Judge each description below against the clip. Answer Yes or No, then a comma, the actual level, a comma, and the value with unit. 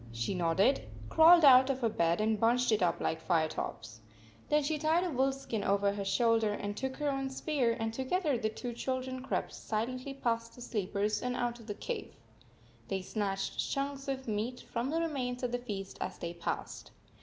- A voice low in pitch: No, high, 240 Hz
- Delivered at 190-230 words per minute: Yes, average, 200 wpm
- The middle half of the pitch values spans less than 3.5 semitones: No, average, 4.6 semitones